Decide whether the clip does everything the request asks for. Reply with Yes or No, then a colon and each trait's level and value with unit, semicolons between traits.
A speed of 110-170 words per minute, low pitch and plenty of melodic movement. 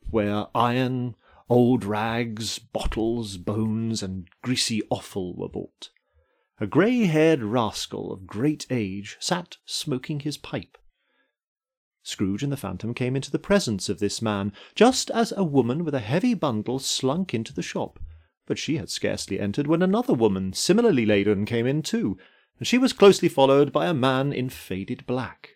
Yes: average, 160 wpm; low, 125 Hz; wide, 6.7 semitones